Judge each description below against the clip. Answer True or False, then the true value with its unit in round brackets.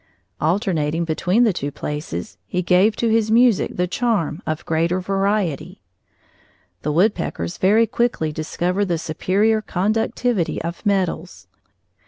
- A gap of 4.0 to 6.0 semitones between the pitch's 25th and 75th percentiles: True (4.9 semitones)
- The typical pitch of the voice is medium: True (180 Hz)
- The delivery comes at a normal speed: False (125 wpm)